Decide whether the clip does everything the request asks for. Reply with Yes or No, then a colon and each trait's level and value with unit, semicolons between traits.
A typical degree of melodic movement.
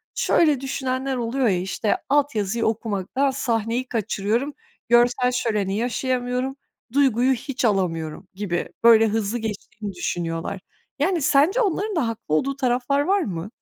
Yes: average, 4.6 semitones